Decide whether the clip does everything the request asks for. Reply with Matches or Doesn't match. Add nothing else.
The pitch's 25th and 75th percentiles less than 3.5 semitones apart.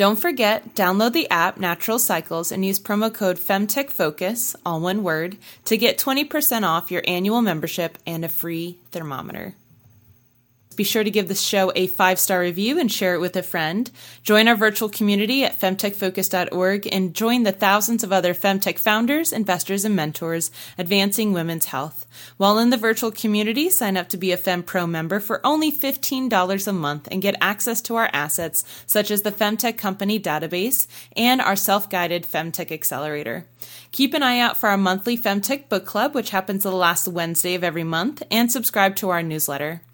Doesn't match